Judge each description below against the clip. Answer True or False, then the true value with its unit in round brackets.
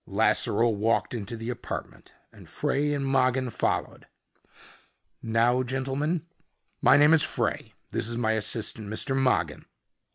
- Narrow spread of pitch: False (3.1 semitones)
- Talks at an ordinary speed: False (130 wpm)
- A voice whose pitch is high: False (125 Hz)